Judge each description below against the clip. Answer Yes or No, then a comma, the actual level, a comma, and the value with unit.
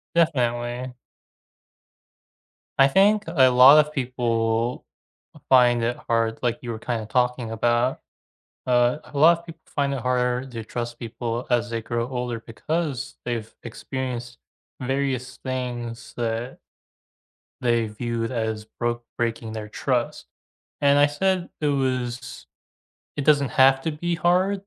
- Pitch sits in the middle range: No, low, 125 Hz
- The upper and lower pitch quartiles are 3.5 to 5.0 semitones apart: No, average, 2.7 semitones